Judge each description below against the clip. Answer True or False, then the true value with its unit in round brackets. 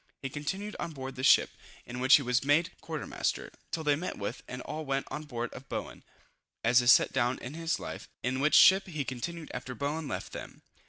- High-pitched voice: False (140 Hz)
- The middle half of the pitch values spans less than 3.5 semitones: False (3.9 semitones)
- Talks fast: True (220 wpm)